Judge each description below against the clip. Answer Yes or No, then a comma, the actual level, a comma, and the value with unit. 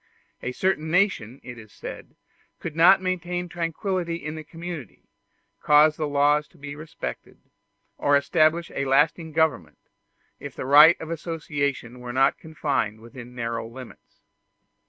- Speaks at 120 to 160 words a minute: Yes, average, 140 wpm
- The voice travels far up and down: No, average, 3.9 semitones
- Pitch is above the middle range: No, medium, 150 Hz